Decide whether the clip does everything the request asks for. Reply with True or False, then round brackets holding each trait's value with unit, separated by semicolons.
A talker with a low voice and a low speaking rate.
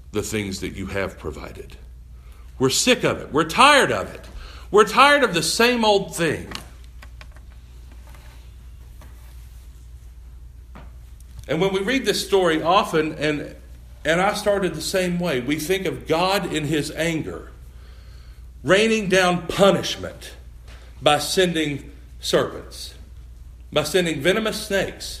True (95 Hz; 125 wpm)